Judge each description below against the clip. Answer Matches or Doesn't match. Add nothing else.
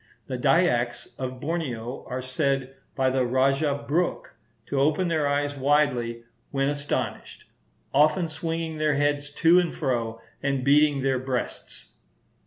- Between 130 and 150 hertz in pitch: Matches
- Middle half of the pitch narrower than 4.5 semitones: Matches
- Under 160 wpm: Matches